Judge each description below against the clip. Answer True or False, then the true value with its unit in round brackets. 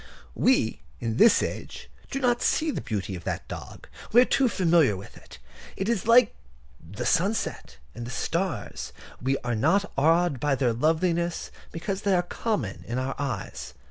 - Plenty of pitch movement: True (8.6 semitones)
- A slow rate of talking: False (175 wpm)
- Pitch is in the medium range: True (165 Hz)